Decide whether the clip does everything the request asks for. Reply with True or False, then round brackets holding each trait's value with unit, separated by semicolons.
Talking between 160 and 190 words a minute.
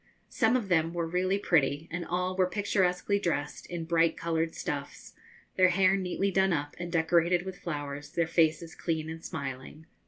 True (175 wpm)